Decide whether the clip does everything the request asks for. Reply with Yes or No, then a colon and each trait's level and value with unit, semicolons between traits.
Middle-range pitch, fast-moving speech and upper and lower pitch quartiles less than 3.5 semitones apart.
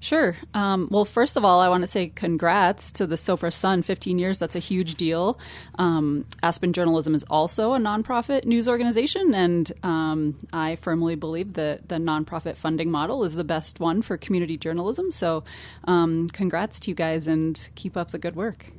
No: medium, 175 Hz; average, 190 wpm; average, 3.1 semitones